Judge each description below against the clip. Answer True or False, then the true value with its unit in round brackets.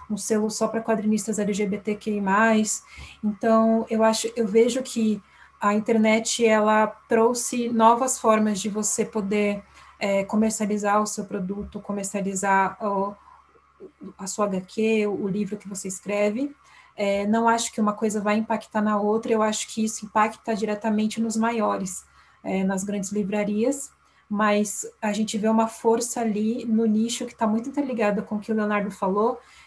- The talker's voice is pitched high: True (215 Hz)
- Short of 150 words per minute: False (155 wpm)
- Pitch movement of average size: False (1.5 semitones)